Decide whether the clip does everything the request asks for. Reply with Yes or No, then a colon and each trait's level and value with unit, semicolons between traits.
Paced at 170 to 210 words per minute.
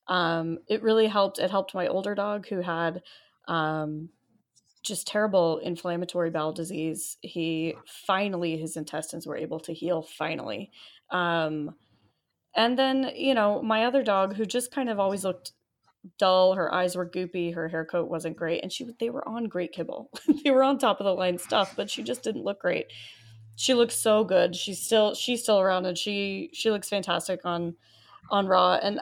Yes: average, 185 wpm